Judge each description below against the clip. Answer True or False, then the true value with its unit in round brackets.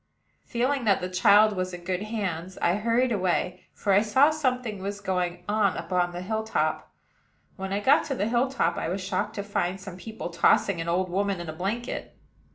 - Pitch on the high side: True (200 Hz)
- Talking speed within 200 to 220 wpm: True (205 wpm)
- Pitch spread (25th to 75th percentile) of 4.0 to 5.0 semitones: False (3.3 semitones)